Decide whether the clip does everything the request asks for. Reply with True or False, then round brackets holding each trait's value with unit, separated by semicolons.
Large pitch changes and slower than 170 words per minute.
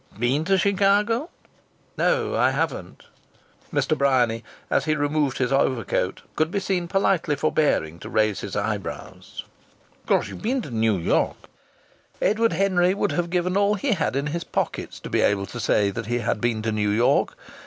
False (8.9 semitones; 175 wpm)